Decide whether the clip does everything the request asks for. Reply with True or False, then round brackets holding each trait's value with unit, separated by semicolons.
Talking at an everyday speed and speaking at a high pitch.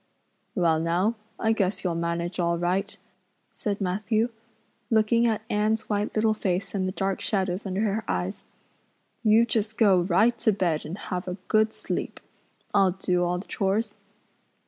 True (160 wpm; 195 Hz)